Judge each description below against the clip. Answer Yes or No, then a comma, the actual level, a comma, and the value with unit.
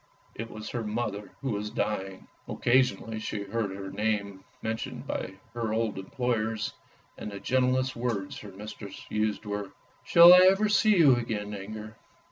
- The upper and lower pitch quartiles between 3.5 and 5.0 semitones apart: No, average, 2.9 semitones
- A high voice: No, low, 110 Hz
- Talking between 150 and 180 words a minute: Yes, average, 160 wpm